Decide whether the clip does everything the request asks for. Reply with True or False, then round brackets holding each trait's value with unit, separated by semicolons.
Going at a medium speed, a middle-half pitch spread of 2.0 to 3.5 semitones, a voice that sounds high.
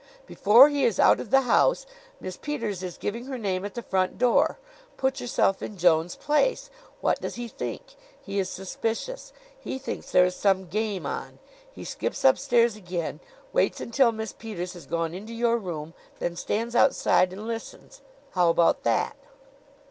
False (170 wpm; 4.8 semitones; 215 Hz)